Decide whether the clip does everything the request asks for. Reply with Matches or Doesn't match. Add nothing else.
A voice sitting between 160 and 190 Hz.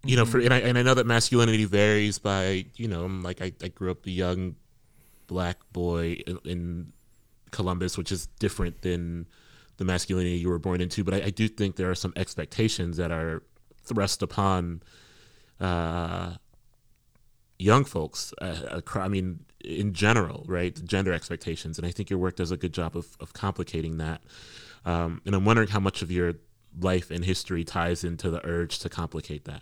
Doesn't match